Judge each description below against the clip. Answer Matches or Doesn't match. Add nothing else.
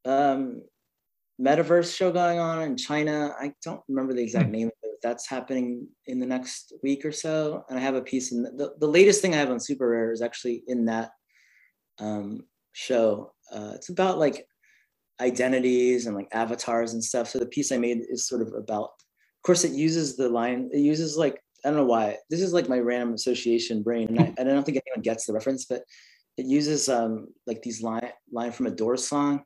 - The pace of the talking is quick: Matches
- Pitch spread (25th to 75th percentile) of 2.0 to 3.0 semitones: Doesn't match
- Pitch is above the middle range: Doesn't match